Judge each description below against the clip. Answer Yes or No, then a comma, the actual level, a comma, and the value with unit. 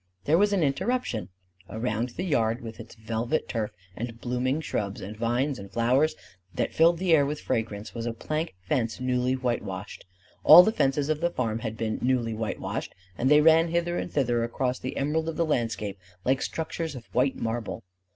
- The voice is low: Yes, low, 125 Hz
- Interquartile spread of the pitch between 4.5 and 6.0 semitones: Yes, average, 5.3 semitones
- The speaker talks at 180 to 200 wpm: Yes, average, 190 wpm